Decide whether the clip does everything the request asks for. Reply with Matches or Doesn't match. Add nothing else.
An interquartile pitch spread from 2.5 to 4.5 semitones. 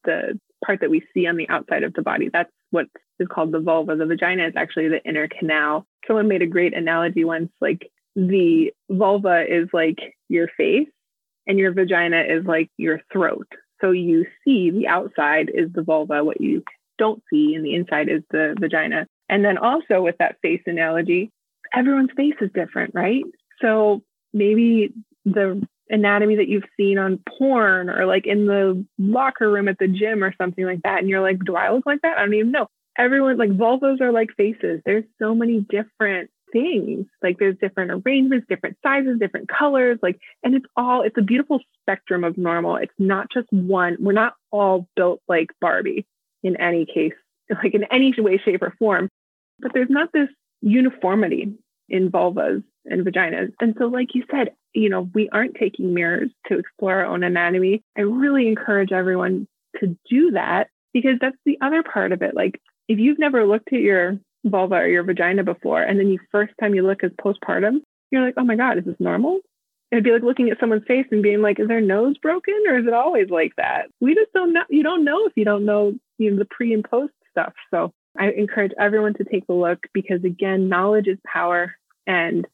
Doesn't match